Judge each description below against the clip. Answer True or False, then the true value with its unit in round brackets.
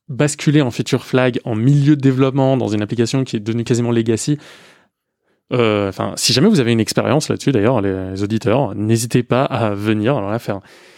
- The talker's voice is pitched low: True (120 Hz)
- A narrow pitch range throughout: False (3.6 semitones)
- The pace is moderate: True (190 wpm)